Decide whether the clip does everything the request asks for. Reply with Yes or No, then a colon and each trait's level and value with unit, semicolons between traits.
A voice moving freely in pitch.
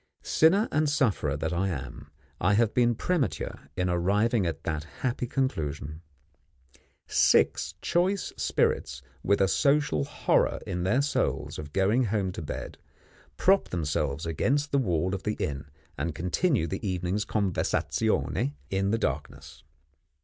Yes: wide, 7.4 semitones